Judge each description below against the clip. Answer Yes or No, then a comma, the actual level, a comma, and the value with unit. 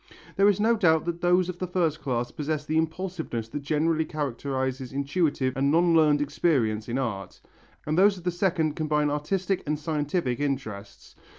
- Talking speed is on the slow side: No, average, 175 wpm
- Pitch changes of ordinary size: Yes, average, 4.1 semitones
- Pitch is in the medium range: Yes, medium, 155 Hz